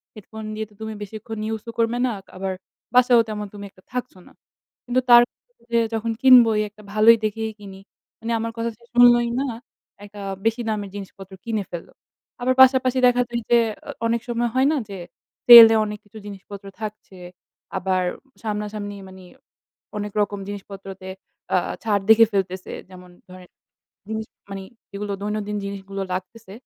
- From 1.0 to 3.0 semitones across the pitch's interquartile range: Yes, average, 2.7 semitones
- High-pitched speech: Yes, high, 215 Hz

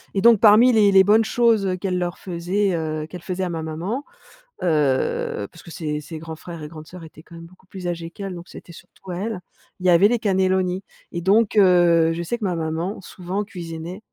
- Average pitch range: Yes, average, 3.0 semitones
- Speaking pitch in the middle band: Yes, medium, 180 Hz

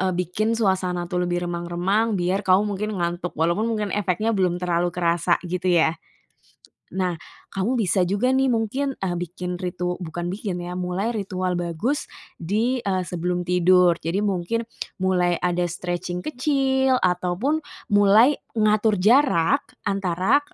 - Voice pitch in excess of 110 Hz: Yes, medium, 185 Hz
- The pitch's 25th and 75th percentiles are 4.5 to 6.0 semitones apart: No, average, 3.4 semitones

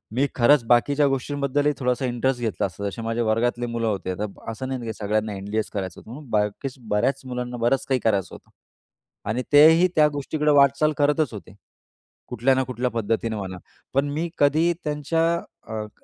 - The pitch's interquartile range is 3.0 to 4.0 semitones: No, average, 4.5 semitones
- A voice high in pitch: No, low, 125 Hz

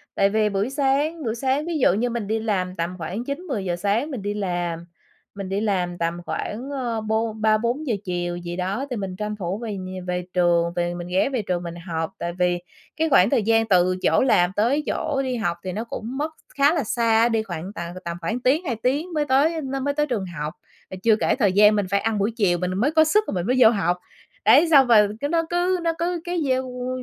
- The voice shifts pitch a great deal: Yes, wide, 6.6 semitones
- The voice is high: Yes, high, 220 Hz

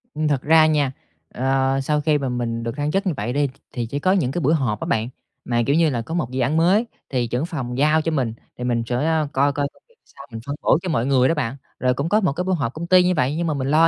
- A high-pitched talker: No, medium, 140 Hz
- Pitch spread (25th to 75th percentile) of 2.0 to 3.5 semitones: No, average, 4.2 semitones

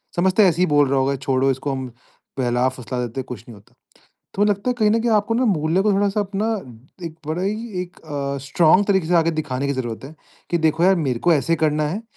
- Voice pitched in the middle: Yes, medium, 160 Hz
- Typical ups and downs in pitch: No, wide, 6.6 semitones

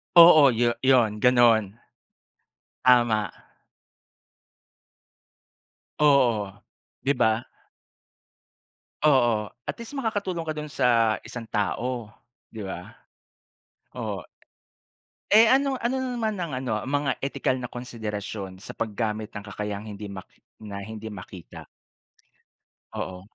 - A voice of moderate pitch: No, low, 120 Hz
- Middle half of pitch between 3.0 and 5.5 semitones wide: Yes, average, 5.1 semitones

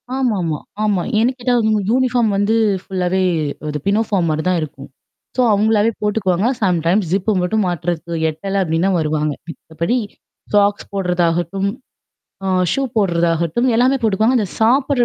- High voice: Yes, high, 195 Hz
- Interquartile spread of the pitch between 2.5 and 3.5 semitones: No, average, 4.4 semitones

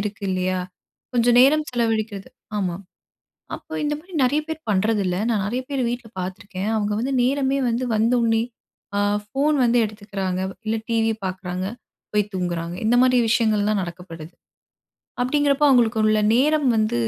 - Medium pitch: No, high, 220 Hz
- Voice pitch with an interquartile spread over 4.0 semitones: Yes, average, 4.4 semitones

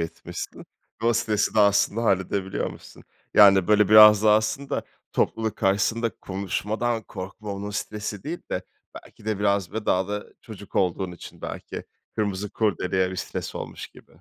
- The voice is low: Yes, low, 105 Hz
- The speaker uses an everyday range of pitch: No, narrow, 2.1 semitones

